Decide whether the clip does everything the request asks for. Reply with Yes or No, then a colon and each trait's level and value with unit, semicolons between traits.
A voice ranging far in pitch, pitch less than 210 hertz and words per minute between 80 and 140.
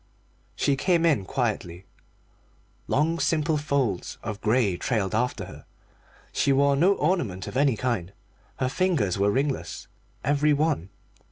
Yes: wide, 6.2 semitones; low, 135 Hz; slow, 135 wpm